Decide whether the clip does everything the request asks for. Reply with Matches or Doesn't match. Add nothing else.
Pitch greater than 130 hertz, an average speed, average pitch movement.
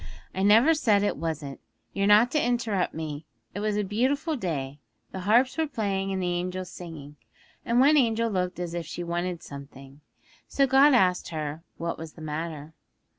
Doesn't match